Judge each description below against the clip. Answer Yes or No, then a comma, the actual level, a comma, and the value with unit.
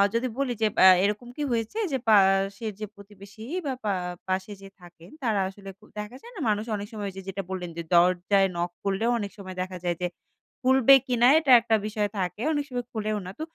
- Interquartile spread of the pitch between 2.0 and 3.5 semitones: Yes, average, 3.2 semitones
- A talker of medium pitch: No, high, 205 Hz